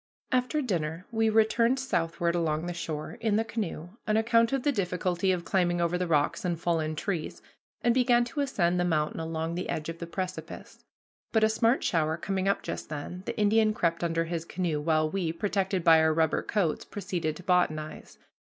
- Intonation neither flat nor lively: Yes, average, 4.8 semitones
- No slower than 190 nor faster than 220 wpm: Yes, average, 195 wpm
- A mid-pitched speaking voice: Yes, medium, 175 Hz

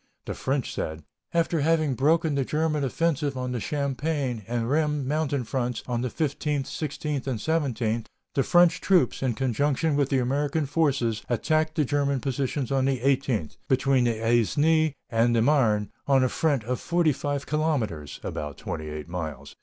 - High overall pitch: No, low, 135 Hz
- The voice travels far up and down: No, average, 3.9 semitones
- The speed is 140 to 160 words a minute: No, average, 170 wpm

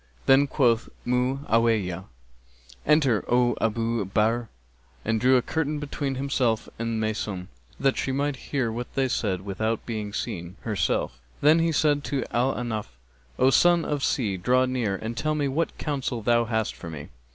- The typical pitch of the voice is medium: No, low, 120 Hz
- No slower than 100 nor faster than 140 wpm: No, average, 170 wpm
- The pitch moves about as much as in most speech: Yes, average, 3.9 semitones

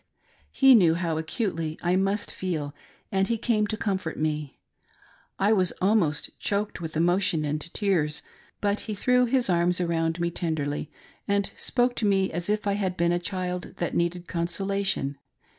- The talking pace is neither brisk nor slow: Yes, average, 165 wpm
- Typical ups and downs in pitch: Yes, average, 3.6 semitones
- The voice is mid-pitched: Yes, medium, 180 Hz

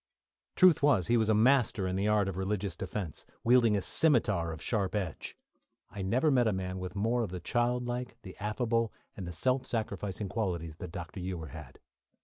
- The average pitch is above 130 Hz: No, low, 105 Hz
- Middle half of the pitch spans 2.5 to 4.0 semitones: No, average, 4.6 semitones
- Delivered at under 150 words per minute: No, average, 190 wpm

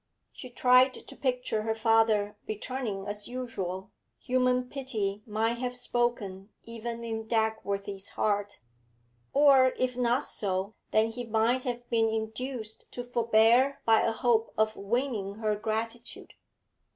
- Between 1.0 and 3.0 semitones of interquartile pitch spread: Yes, narrow, 2.6 semitones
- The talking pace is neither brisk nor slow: No, slow, 130 wpm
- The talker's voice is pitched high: Yes, high, 225 Hz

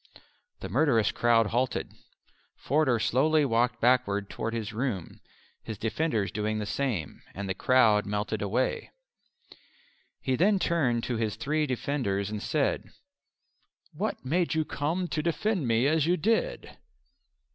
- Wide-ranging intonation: Yes, wide, 5.9 semitones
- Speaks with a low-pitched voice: Yes, low, 125 Hz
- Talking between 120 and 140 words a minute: Yes, slow, 135 wpm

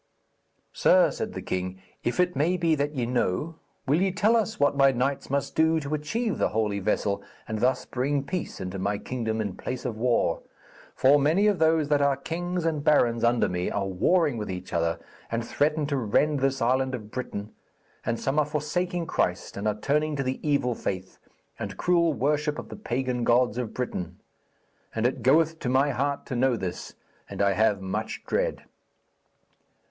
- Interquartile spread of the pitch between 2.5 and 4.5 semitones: No, wide, 5.5 semitones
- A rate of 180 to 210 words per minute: Yes, average, 190 wpm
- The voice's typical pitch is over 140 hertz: No, low, 135 Hz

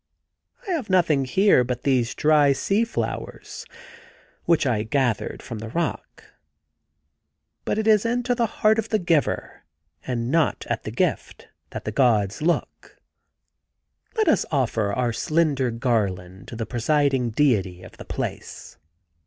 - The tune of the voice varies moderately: No, wide, 7.0 semitones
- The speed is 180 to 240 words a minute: No, average, 145 wpm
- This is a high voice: No, low, 135 Hz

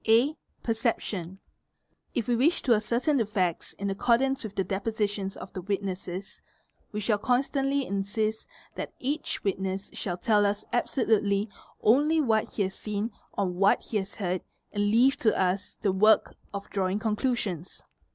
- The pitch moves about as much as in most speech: Yes, average, 3.2 semitones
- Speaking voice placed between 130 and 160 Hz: No, high, 210 Hz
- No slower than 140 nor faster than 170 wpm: Yes, average, 160 wpm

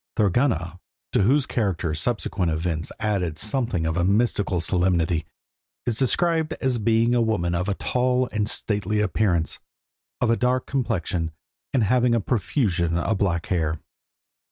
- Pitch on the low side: Yes, low, 105 Hz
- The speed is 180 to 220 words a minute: No, average, 145 wpm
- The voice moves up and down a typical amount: No, wide, 5.8 semitones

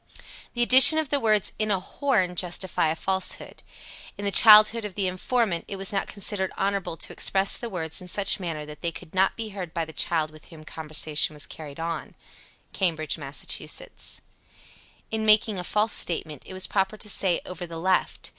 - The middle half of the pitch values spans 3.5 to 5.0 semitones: Yes, average, 4.3 semitones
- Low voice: No, high, 190 Hz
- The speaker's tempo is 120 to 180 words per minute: No, average, 200 wpm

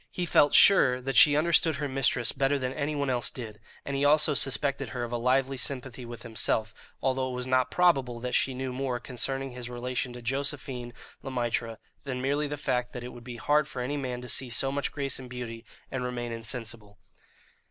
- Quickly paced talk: Yes, fast, 210 wpm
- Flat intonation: Yes, narrow, 2.2 semitones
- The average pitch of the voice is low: Yes, low, 130 Hz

